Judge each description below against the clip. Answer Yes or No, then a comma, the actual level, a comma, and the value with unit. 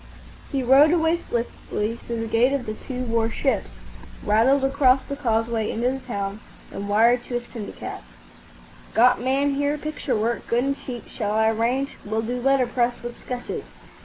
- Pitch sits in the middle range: No, high, 245 Hz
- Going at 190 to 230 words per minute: No, average, 170 wpm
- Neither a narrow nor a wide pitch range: Yes, average, 3.0 semitones